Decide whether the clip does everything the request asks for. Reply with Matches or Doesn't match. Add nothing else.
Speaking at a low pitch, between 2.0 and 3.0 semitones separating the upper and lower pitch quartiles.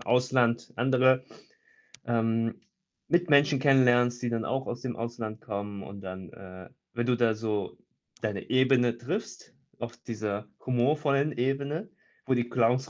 Matches